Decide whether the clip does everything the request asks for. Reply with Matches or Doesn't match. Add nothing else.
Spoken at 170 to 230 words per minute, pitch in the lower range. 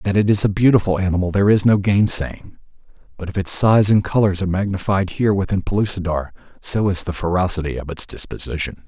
Matches